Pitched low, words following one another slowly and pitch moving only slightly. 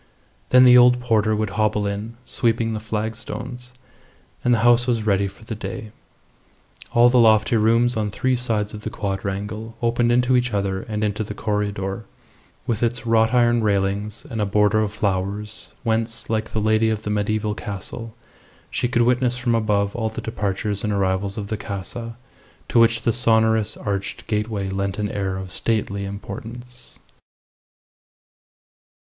No: low, 110 Hz; average, 165 wpm; narrow, 2.3 semitones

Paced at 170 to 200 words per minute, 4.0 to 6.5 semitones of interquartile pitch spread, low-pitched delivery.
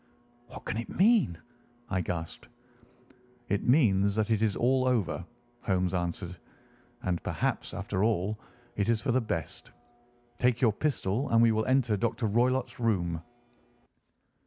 No: average, 140 wpm; average, 4.6 semitones; low, 110 Hz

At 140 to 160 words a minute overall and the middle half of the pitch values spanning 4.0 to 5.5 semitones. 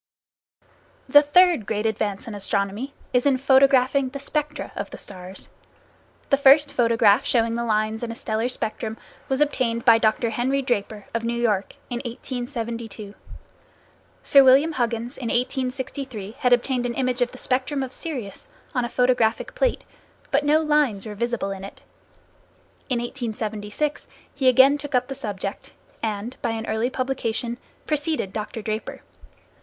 No: average, 155 wpm; average, 3.4 semitones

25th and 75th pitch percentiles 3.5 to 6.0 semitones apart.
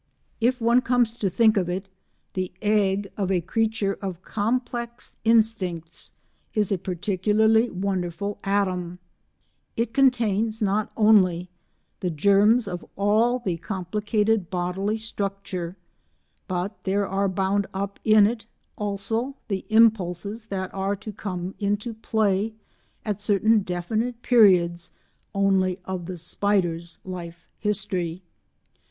No: average, 3.0 semitones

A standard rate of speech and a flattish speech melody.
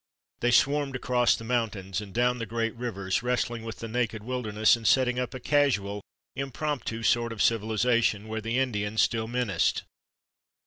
Yes: average, 165 wpm; narrow, 2.3 semitones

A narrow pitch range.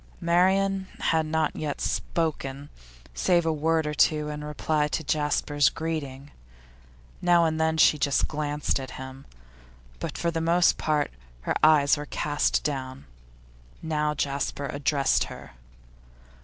Yes: narrow, 2.0 semitones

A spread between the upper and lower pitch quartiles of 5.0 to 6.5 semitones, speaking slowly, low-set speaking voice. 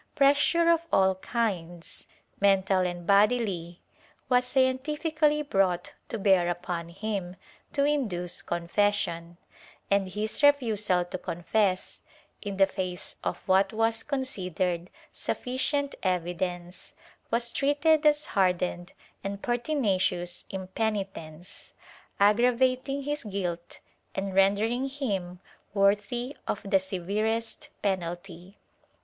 No: wide, 5.6 semitones; slow, 100 wpm; high, 200 Hz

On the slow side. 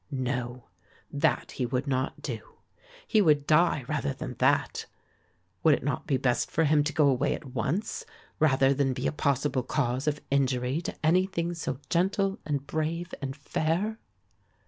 No: average, 165 wpm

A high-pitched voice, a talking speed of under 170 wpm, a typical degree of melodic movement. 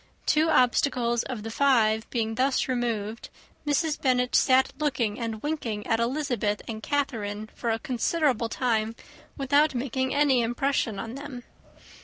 Yes: high, 245 Hz; average, 140 wpm; average, 3.6 semitones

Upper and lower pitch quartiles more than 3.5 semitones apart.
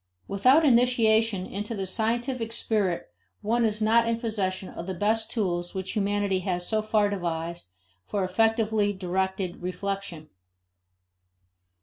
No: average, 3.2 semitones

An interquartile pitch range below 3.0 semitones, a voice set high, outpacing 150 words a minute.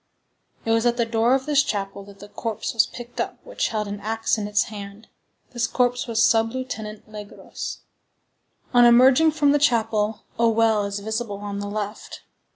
Yes: narrow, 2.6 semitones; high, 225 Hz; average, 185 wpm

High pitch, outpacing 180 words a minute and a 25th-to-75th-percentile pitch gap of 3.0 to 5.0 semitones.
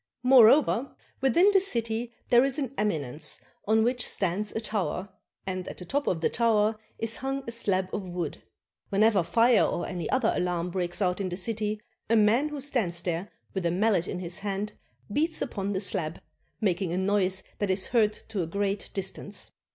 Yes: high, 205 Hz; average, 190 wpm; average, 4.0 semitones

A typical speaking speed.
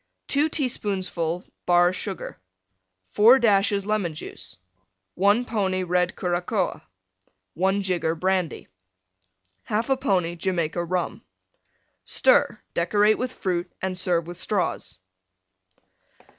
No: slow, 100 wpm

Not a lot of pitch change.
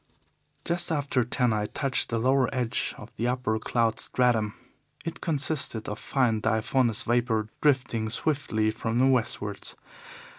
No: average, 3.2 semitones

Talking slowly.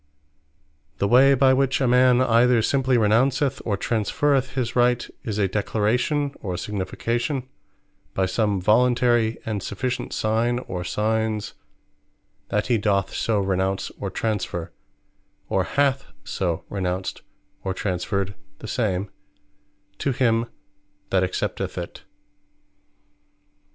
Yes: slow, 115 wpm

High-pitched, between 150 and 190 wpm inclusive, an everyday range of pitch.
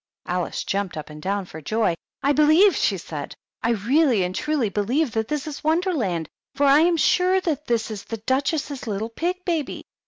No: very high, 250 Hz; average, 185 wpm; wide, 7.4 semitones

